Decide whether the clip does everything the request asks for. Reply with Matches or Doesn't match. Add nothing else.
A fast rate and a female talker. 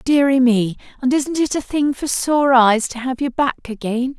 Matches